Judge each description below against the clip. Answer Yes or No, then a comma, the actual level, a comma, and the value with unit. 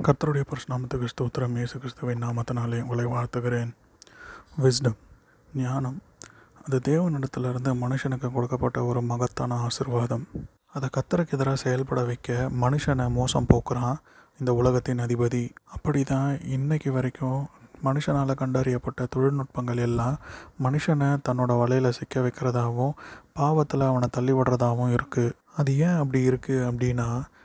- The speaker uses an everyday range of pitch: No, narrow, 1.9 semitones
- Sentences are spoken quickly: No, average, 110 wpm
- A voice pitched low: Yes, low, 130 Hz